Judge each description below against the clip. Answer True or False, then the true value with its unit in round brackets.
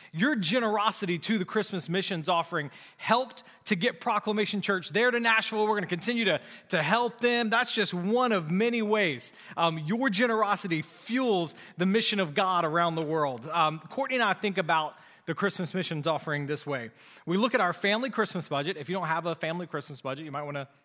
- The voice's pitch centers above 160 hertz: True (190 Hz)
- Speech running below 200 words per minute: False (205 wpm)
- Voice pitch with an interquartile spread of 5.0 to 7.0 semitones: True (5.3 semitones)